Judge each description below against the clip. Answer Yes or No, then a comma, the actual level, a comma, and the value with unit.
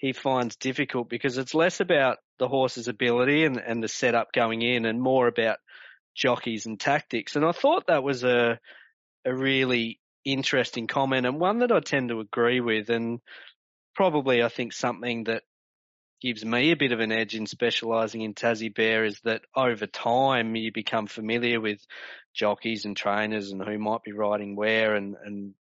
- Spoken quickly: No, average, 180 wpm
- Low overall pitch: Yes, low, 115 Hz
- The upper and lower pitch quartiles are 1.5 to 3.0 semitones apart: Yes, narrow, 2.4 semitones